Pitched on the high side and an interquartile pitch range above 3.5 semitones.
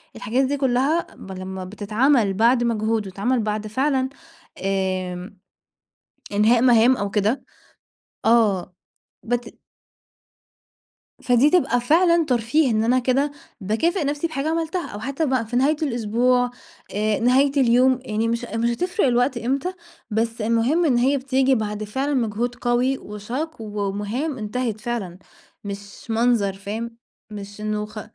Yes: high, 235 Hz; average, 3.9 semitones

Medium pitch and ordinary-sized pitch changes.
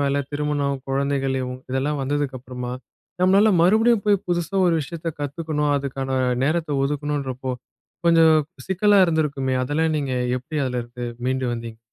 Yes: medium, 145 Hz; average, 3.7 semitones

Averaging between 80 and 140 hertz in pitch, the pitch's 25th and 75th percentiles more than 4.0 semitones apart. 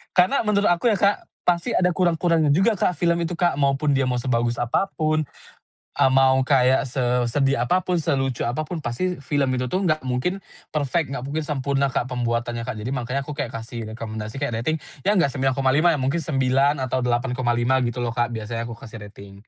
Yes: low, 135 Hz; average, 4.7 semitones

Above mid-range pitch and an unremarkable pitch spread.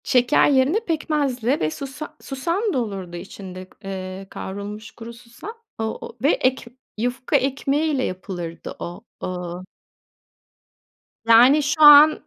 No: high, 245 Hz; wide, 6.7 semitones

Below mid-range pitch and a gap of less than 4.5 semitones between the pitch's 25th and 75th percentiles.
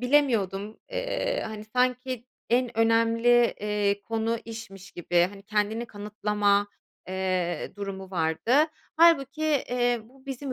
No: high, 225 Hz; average, 3.7 semitones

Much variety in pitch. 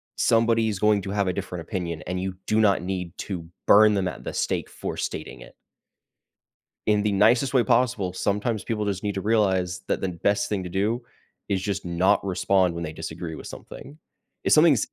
No: average, 2.9 semitones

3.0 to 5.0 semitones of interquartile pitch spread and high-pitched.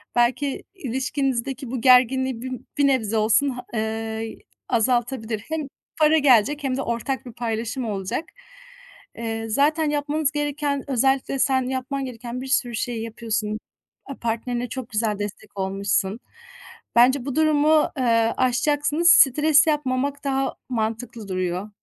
Yes: average, 3.7 semitones; very high, 250 Hz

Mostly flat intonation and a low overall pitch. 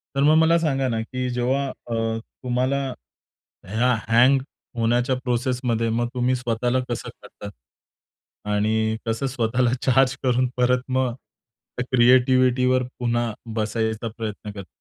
Yes: narrow, 2.1 semitones; low, 125 Hz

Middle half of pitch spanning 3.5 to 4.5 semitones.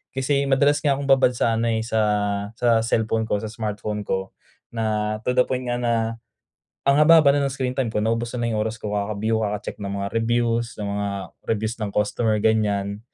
No: average, 2.9 semitones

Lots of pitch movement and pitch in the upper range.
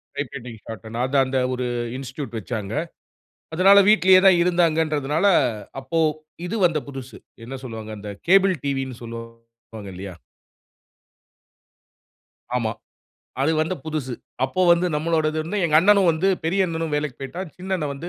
No: wide, 5.9 semitones; medium, 150 Hz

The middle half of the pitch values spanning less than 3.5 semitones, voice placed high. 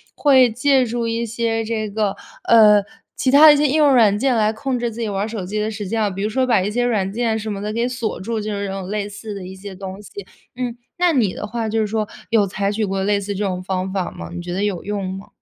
Yes: average, 2.8 semitones; high, 215 Hz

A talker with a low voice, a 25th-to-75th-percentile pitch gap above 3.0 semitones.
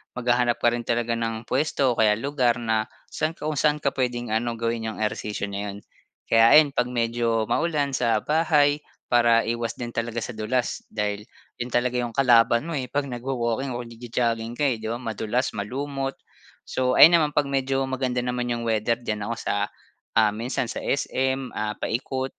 No: low, 120 Hz; narrow, 2.6 semitones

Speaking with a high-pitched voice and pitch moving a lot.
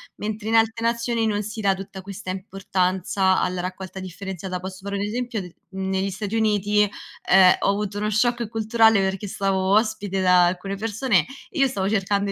No: high, 200 Hz; narrow, 2.4 semitones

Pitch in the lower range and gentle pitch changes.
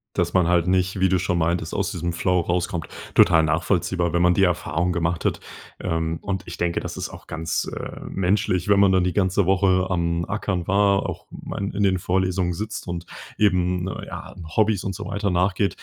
Yes: very low, 90 Hz; narrow, 2.0 semitones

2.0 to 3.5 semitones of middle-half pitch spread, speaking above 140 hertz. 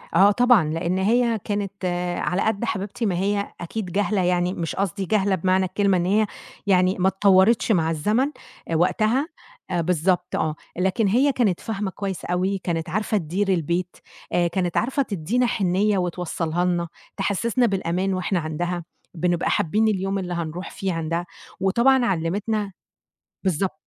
Yes: average, 2.9 semitones; high, 190 Hz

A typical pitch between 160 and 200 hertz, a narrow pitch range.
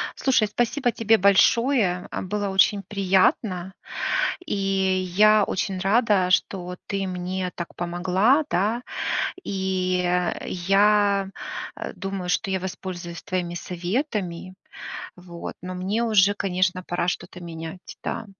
Yes: high, 190 Hz; narrow, 2.2 semitones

